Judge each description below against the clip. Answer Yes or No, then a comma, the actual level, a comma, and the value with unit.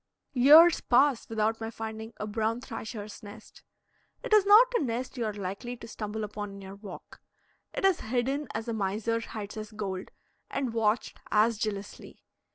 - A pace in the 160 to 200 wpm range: Yes, average, 170 wpm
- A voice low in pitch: No, high, 225 Hz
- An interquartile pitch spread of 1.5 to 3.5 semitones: Yes, average, 2.7 semitones